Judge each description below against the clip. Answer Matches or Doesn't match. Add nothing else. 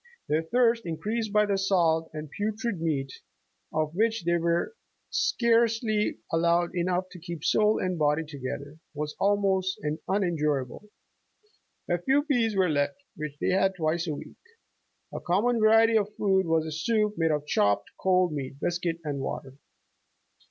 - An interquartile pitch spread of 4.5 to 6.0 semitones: Matches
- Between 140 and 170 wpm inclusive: Matches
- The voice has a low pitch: Doesn't match